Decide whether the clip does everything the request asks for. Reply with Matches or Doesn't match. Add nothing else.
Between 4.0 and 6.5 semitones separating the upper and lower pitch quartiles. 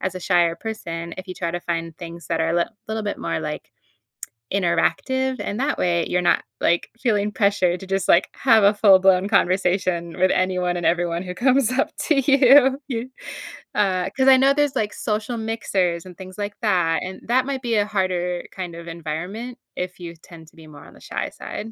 Matches